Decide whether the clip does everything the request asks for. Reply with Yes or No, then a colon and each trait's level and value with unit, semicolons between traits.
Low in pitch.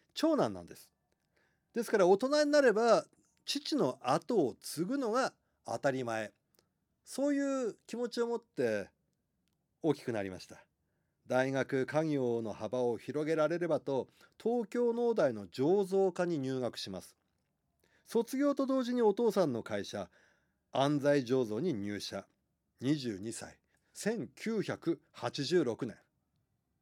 No: medium, 155 Hz